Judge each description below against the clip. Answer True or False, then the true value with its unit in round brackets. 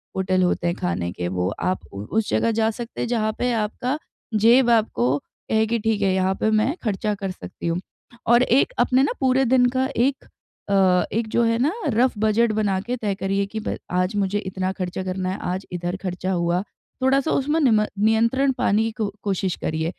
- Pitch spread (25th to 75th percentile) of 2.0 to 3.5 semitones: False (4.0 semitones)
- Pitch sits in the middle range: False (210 Hz)